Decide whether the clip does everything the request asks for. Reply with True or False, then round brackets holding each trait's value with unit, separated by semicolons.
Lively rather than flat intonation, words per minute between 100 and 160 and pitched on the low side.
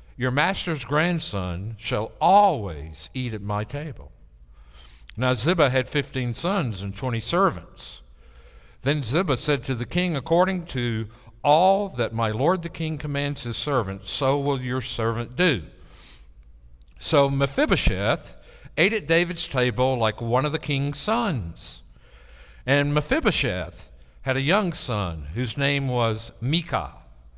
True (7.3 semitones; 135 wpm; 125 Hz)